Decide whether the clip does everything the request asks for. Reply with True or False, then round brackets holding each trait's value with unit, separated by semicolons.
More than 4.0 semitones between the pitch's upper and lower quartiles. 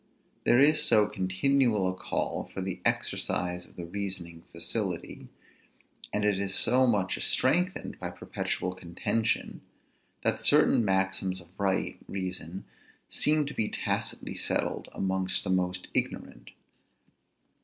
False (3.0 semitones)